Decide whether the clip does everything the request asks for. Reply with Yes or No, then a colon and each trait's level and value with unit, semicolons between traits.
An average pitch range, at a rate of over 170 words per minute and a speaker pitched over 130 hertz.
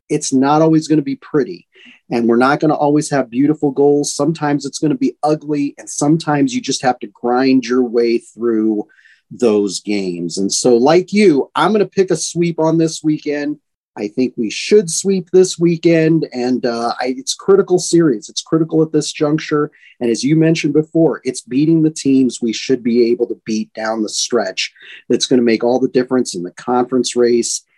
Yes: average, 4.4 semitones; fast, 205 wpm; medium, 140 Hz